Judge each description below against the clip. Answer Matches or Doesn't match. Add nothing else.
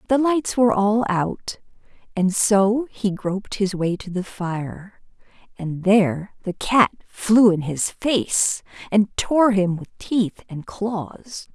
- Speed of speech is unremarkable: Matches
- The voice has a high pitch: Matches